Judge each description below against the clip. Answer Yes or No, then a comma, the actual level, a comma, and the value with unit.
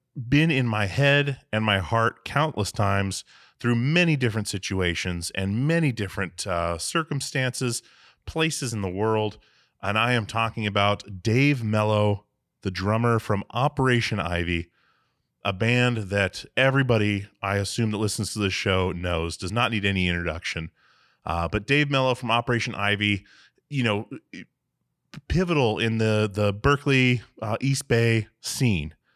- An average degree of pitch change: Yes, average, 4.1 semitones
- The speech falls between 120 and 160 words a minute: Yes, average, 140 wpm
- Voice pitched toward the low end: Yes, low, 110 Hz